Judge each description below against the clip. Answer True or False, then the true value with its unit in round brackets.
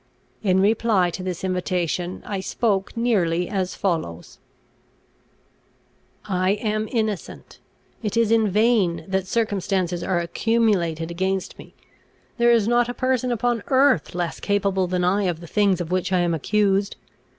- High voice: True (195 Hz)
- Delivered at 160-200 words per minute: False (145 wpm)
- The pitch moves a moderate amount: True (3.6 semitones)